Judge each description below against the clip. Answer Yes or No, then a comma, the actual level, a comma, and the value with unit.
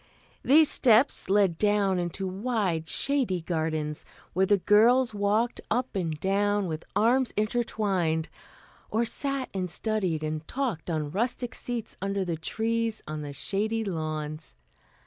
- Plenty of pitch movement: Yes, wide, 5.7 semitones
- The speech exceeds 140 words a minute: No, slow, 135 wpm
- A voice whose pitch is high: Yes, high, 200 Hz